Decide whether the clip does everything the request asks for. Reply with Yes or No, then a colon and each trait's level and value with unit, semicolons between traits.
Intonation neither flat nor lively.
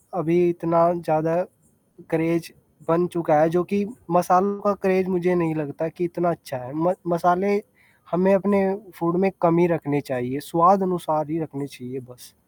No: narrow, 2.3 semitones